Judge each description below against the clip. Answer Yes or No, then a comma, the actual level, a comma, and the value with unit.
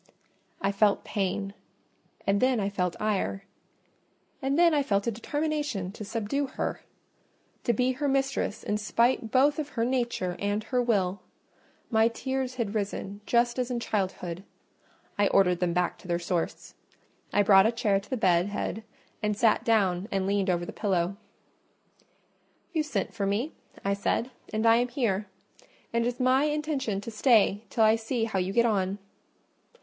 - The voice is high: Yes, high, 215 Hz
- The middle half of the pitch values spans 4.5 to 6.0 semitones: No, average, 4.1 semitones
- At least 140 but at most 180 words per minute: Yes, average, 170 wpm